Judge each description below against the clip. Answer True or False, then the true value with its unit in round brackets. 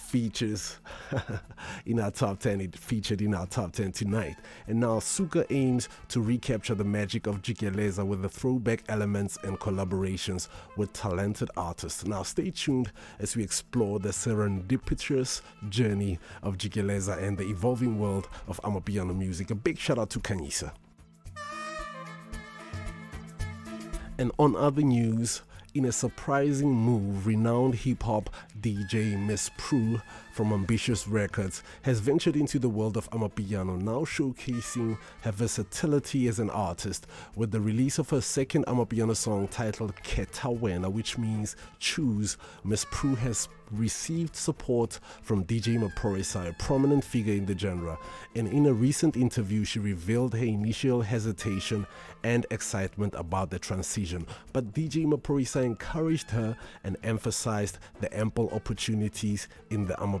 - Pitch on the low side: True (110 Hz)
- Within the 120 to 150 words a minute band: True (140 wpm)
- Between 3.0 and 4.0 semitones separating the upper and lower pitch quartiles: True (3.6 semitones)